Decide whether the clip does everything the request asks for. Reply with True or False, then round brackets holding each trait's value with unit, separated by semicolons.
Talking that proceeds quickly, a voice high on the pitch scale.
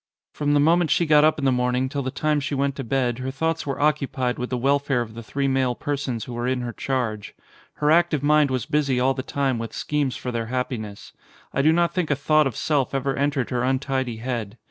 False (240 wpm; 135 Hz)